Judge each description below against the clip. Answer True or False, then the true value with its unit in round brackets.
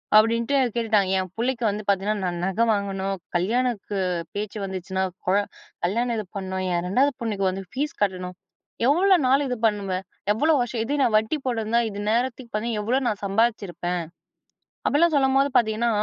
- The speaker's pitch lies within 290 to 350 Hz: False (215 Hz)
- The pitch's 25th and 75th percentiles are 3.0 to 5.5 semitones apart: True (4.0 semitones)